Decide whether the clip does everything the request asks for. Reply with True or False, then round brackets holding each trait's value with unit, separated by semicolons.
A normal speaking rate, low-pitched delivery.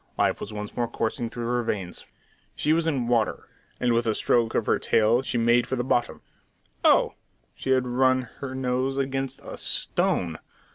True (185 wpm; 120 Hz)